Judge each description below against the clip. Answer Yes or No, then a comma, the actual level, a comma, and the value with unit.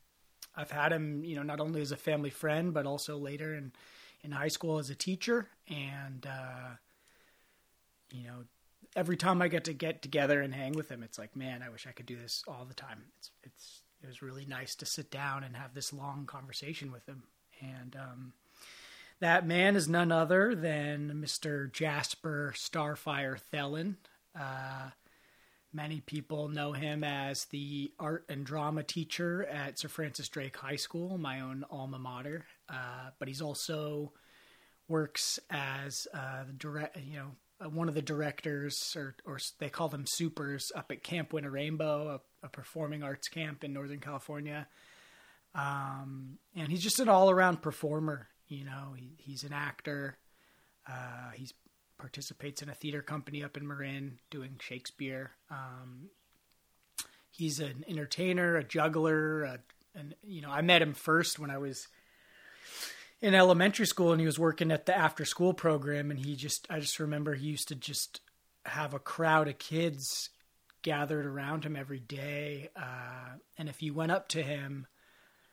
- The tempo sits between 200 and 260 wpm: No, average, 170 wpm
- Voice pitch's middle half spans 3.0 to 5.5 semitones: No, narrow, 2.4 semitones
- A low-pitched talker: No, medium, 145 Hz